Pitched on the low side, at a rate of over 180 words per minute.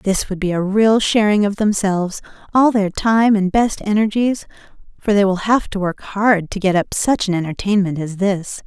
No: high, 200 Hz; average, 200 wpm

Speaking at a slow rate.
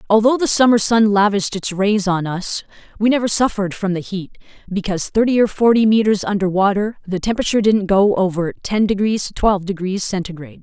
No: average, 180 wpm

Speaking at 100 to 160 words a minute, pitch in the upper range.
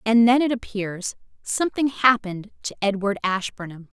Yes: slow, 135 wpm; high, 215 Hz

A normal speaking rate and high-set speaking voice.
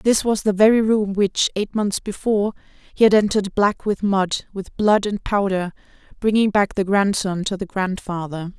Yes: average, 180 wpm; high, 200 Hz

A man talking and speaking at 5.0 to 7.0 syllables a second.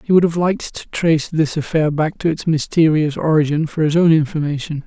Yes: male; 5.7 syllables/s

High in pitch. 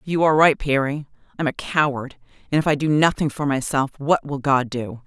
No: medium, 140 Hz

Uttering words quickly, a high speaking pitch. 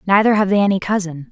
Yes: fast, 225 wpm; high, 195 Hz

